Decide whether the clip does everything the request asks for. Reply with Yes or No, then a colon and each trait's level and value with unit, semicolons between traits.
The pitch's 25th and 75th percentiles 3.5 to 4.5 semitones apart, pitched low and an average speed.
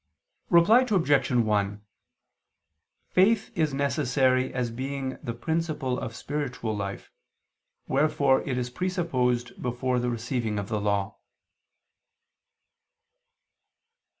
No: average, 4.0 semitones; low, 130 Hz; slow, 95 wpm